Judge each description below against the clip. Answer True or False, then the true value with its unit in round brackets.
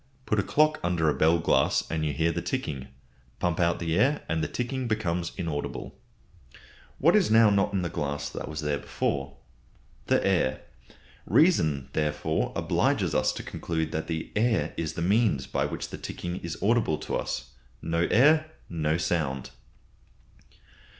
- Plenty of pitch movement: True (5.7 semitones)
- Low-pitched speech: True (85 Hz)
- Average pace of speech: True (160 wpm)